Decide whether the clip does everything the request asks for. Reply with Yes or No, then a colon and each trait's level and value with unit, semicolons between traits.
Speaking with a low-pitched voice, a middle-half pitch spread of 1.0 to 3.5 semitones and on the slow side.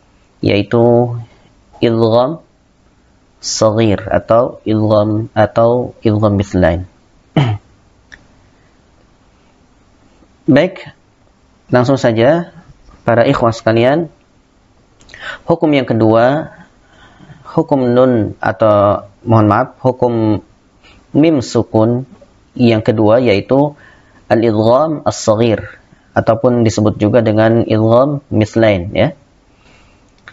Yes: low, 115 Hz; average, 2.7 semitones; slow, 70 wpm